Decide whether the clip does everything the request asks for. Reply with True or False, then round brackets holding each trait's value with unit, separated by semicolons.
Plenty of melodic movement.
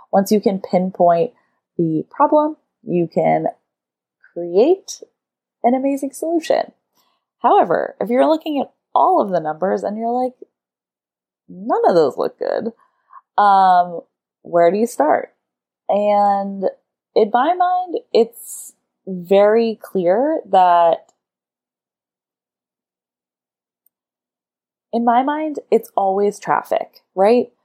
True (8.9 semitones)